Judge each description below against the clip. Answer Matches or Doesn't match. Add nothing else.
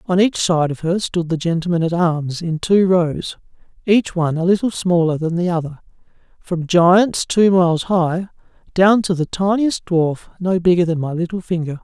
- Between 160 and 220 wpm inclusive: Matches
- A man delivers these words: Matches